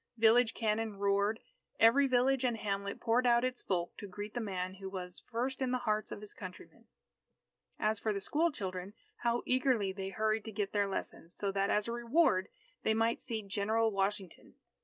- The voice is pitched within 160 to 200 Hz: No, high, 215 Hz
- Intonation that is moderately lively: Yes, average, 3.1 semitones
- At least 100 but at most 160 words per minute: No, average, 190 wpm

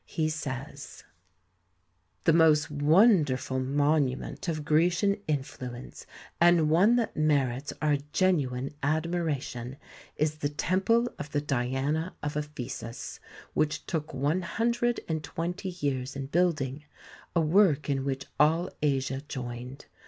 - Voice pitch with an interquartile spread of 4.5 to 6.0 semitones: No, average, 3.7 semitones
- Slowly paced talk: Yes, slow, 125 wpm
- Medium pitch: Yes, medium, 150 Hz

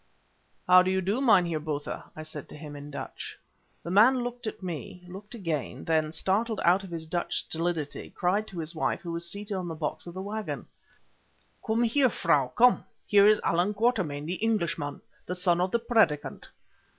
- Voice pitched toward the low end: No, medium, 180 Hz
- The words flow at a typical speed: Yes, average, 190 wpm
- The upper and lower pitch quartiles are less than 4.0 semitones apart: No, average, 4.7 semitones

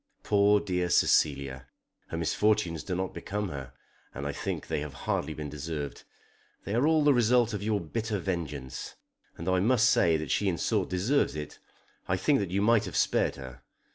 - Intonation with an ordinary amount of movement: No, wide, 5.9 semitones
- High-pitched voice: No, very low, 90 Hz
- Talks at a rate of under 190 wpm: No, average, 195 wpm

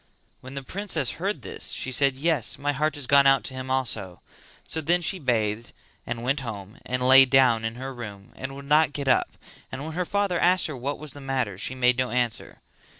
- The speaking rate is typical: No, fast, 220 wpm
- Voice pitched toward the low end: Yes, low, 130 Hz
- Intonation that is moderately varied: Yes, average, 3.1 semitones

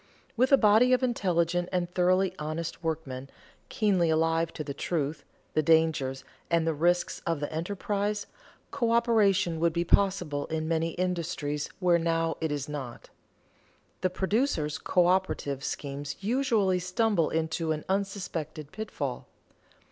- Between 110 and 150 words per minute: Yes, slow, 135 wpm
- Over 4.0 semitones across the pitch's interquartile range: No, average, 3.7 semitones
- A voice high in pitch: No, medium, 170 Hz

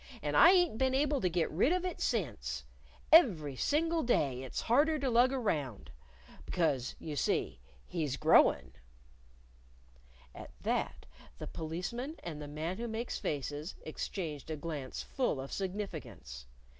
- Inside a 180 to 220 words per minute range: No, average, 145 wpm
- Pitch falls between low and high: Yes, medium, 170 Hz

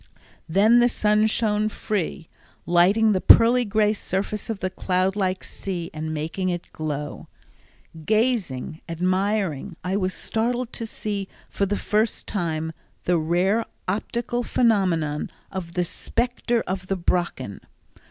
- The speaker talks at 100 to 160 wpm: Yes, slow, 135 wpm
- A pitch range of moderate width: Yes, average, 3.9 semitones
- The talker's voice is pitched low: No, high, 195 Hz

